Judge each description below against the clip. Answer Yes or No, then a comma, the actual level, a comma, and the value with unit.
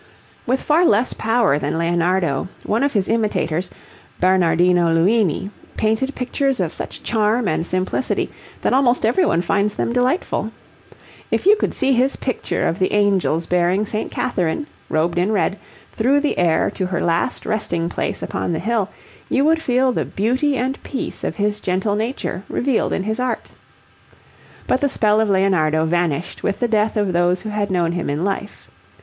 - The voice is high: Yes, high, 205 Hz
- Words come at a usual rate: Yes, average, 170 wpm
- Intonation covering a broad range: Yes, wide, 5.7 semitones